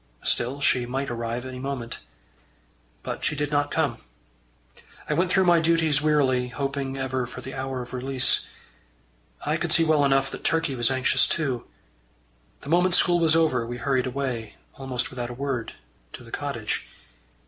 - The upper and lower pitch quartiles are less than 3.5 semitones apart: Yes, average, 3.1 semitones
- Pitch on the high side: No, low, 135 Hz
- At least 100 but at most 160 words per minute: No, average, 170 wpm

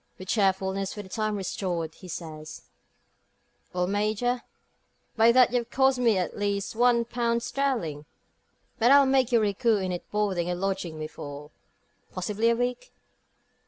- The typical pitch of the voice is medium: No, high, 205 Hz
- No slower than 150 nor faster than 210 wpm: Yes, average, 160 wpm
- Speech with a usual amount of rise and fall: Yes, average, 4.5 semitones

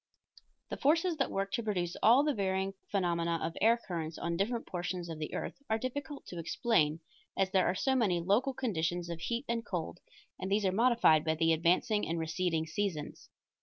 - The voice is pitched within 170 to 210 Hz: Yes, high, 190 Hz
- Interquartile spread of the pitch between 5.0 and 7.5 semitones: Yes, wide, 5.5 semitones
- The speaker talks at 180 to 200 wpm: Yes, average, 195 wpm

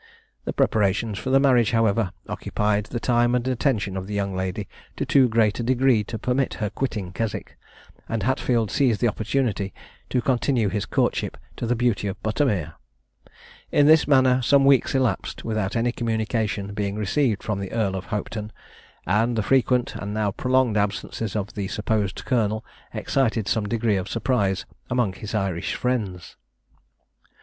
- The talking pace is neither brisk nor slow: Yes, average, 165 wpm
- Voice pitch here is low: Yes, low, 110 Hz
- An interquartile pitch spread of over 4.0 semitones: No, average, 3.5 semitones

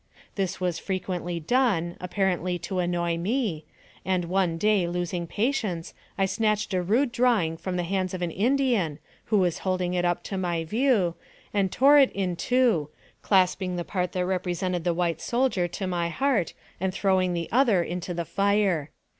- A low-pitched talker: No, medium, 185 Hz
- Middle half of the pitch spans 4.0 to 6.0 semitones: No, average, 3.0 semitones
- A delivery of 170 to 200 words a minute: Yes, average, 175 wpm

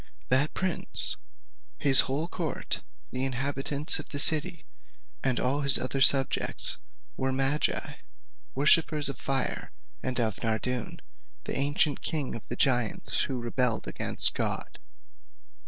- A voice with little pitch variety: Yes, narrow, 2.3 semitones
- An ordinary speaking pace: No, slow, 125 wpm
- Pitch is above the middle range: No, low, 135 Hz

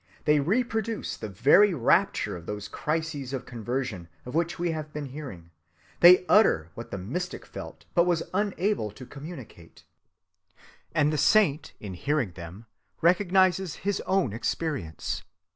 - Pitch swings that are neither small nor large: No, wide, 8.2 semitones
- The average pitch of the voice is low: No, medium, 150 Hz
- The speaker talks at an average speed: Yes, average, 145 wpm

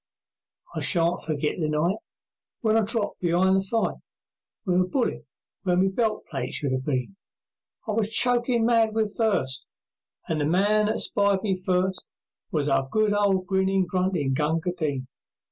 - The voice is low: No, high, 190 Hz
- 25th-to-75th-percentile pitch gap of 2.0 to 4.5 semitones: No, average, 5.0 semitones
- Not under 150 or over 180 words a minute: Yes, average, 160 wpm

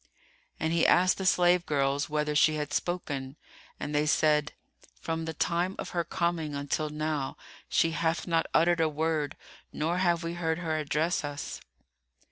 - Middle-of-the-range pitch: Yes, medium, 160 Hz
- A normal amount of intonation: No, narrow, 2.3 semitones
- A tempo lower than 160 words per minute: No, average, 165 wpm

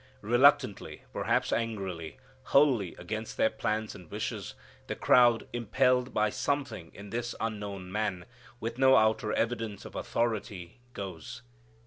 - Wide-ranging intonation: No, average, 3.2 semitones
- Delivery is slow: Yes, slow, 125 wpm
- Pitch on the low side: Yes, low, 110 Hz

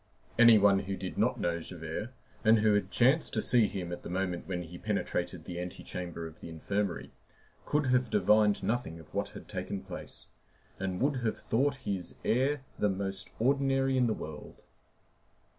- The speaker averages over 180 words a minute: No, average, 175 wpm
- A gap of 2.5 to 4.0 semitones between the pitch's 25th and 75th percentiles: No, average, 5.3 semitones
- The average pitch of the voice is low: Yes, low, 100 Hz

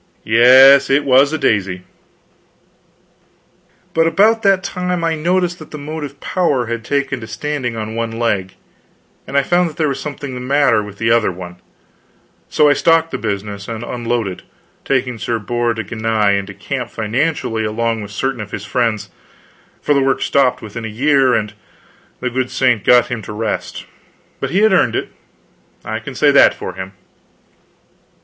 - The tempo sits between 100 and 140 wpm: No, average, 175 wpm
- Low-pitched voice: Yes, low, 125 Hz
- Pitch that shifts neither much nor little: Yes, average, 4.8 semitones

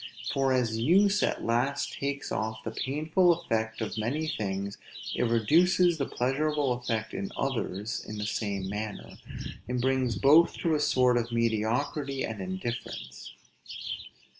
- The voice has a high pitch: No, low, 125 Hz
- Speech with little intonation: No, average, 4.8 semitones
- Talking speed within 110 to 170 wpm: Yes, average, 140 wpm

